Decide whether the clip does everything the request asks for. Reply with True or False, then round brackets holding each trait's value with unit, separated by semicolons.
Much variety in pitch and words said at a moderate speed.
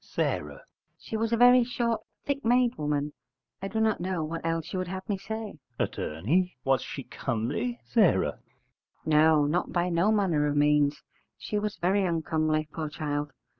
True (6.4 semitones; 170 wpm)